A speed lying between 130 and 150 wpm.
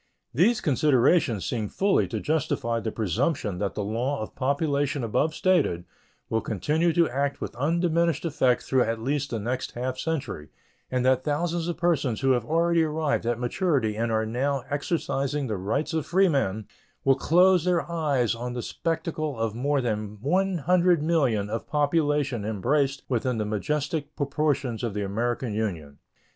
No: average, 160 wpm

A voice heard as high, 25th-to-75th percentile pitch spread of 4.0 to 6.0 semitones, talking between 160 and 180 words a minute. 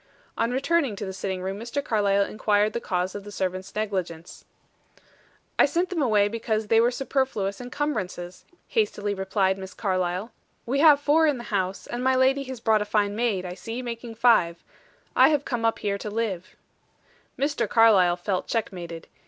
Yes: high, 215 Hz; average, 4.4 semitones; average, 175 wpm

